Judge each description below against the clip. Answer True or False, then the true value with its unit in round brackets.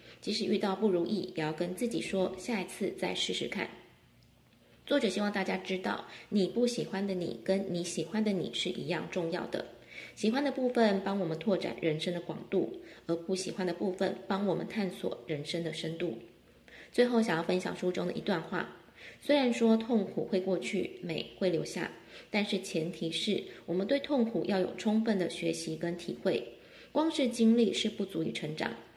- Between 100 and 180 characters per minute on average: False (275 characters per minute)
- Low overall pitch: False (190 Hz)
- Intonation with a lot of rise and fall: False (4.1 semitones)